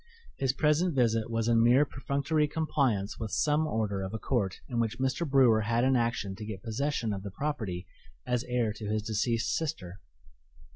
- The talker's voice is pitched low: Yes, low, 115 Hz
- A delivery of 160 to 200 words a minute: Yes, average, 185 wpm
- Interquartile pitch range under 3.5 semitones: No, average, 4.3 semitones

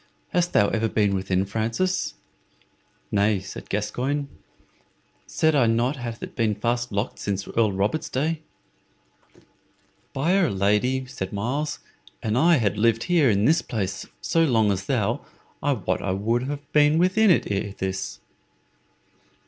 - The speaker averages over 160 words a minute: No, average, 140 wpm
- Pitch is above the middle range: No, low, 115 Hz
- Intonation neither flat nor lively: No, wide, 6.2 semitones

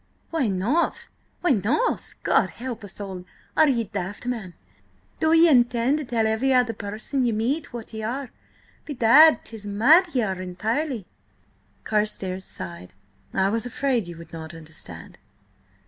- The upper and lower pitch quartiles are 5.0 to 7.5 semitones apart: Yes, average, 5.3 semitones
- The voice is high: Yes, high, 225 Hz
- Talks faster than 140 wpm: Yes, average, 150 wpm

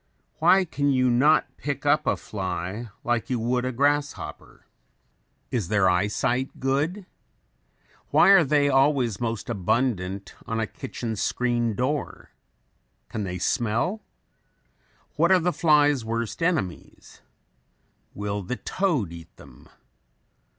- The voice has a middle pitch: No, low, 125 Hz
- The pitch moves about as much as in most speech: No, wide, 5.7 semitones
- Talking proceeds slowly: Yes, slow, 125 wpm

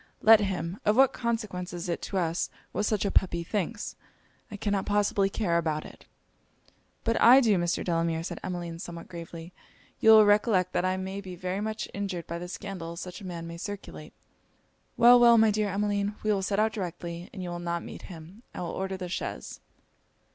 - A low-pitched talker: No, high, 190 Hz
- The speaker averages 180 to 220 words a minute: Yes, average, 200 wpm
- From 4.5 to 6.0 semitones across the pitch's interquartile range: No, average, 3.4 semitones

